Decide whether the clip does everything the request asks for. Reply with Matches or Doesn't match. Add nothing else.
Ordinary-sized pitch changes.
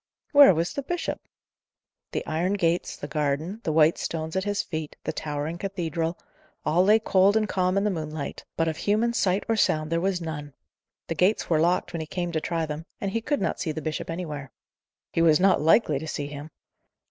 Matches